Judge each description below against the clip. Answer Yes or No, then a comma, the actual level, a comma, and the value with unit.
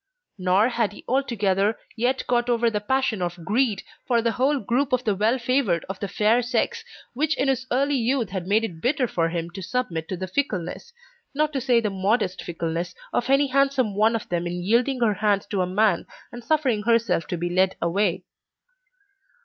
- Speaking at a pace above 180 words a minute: Yes, average, 200 wpm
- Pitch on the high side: Yes, high, 220 Hz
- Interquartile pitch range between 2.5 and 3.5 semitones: No, average, 5.2 semitones